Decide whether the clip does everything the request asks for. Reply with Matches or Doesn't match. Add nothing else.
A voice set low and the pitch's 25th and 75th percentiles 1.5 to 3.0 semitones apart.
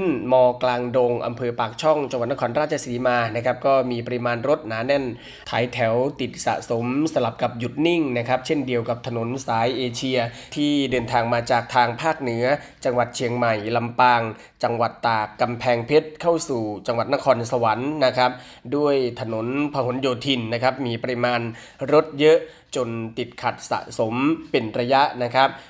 Matches